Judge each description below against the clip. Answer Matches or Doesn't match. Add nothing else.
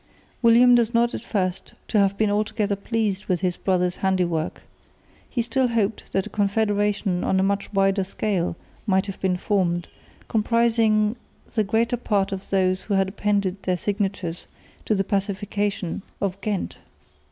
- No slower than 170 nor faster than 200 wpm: Doesn't match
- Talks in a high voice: Matches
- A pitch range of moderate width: Doesn't match